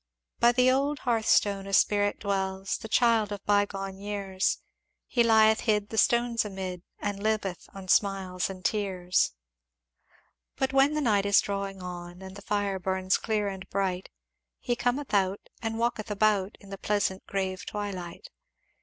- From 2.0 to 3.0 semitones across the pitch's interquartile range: Yes, narrow, 2.4 semitones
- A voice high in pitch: Yes, high, 200 Hz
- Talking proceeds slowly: No, average, 155 wpm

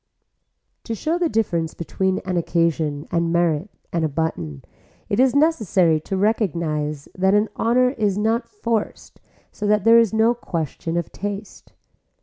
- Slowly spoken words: No, average, 150 wpm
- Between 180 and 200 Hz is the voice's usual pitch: Yes, high, 190 Hz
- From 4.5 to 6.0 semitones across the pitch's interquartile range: Yes, average, 5.3 semitones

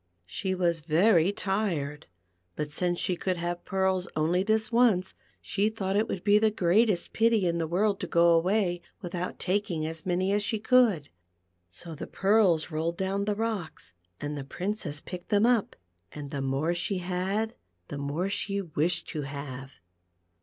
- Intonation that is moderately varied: Yes, average, 4.0 semitones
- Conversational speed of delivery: Yes, average, 170 wpm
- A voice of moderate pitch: Yes, medium, 180 Hz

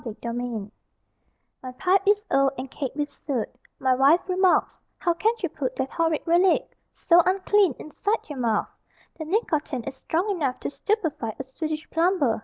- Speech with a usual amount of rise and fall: No, wide, 6.0 semitones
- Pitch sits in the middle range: No, very high, 310 Hz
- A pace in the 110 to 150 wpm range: No, average, 170 wpm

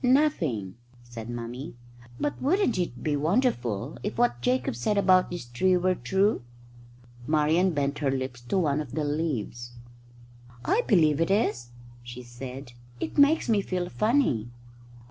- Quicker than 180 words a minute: No, average, 145 wpm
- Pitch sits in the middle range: Yes, medium, 150 Hz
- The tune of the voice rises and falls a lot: Yes, wide, 7.9 semitones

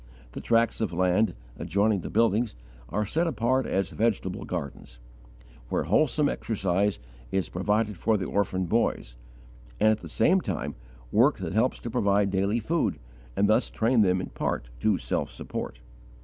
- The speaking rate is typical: Yes, average, 160 wpm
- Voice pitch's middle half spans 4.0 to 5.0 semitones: No, average, 3.4 semitones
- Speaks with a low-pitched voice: Yes, low, 105 Hz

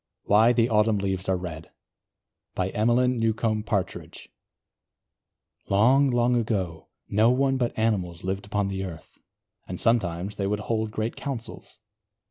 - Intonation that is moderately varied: Yes, average, 3.6 semitones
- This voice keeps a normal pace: No, slow, 130 wpm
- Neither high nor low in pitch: No, low, 105 Hz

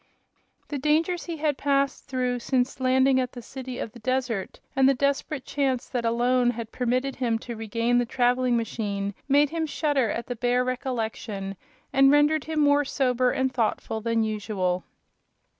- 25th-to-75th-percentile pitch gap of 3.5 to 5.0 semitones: No, average, 2.9 semitones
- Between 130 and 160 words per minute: No, average, 170 wpm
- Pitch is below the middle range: No, very high, 255 Hz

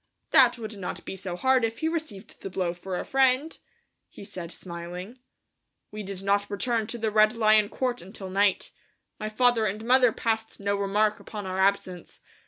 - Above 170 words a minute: Yes, average, 185 wpm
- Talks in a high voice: Yes, high, 210 Hz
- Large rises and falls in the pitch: No, average, 3.3 semitones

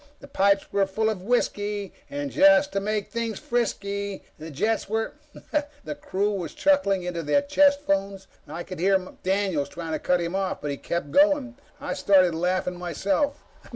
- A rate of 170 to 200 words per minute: Yes, average, 185 wpm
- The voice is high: Yes, high, 200 Hz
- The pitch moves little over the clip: No, average, 5.0 semitones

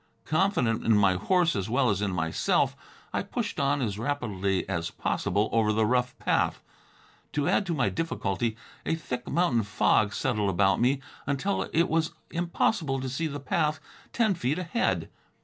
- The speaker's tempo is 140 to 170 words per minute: Yes, average, 165 wpm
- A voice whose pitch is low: Yes, low, 125 Hz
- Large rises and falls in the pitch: Yes, wide, 7.4 semitones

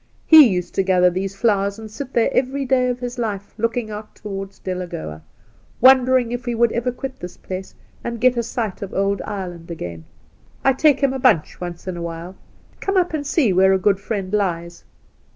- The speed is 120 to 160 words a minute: No, average, 200 wpm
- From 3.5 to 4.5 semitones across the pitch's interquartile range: No, average, 5.2 semitones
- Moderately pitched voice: No, high, 210 Hz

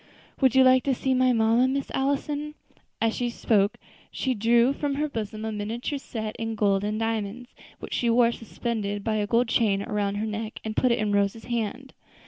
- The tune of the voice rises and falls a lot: No, average, 3.2 semitones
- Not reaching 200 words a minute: No, fast, 205 wpm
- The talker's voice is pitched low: No, high, 230 Hz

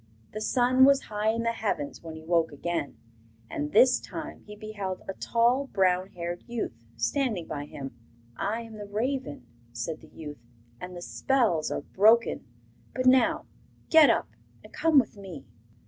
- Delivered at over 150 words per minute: Yes, average, 165 wpm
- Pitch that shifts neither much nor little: No, wide, 6.2 semitones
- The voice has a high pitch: Yes, high, 205 Hz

